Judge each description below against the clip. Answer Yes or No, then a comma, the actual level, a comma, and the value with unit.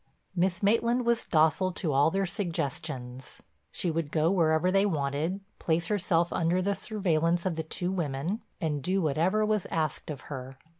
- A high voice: No, medium, 170 Hz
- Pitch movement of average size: Yes, average, 3.7 semitones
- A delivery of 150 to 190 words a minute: Yes, average, 165 wpm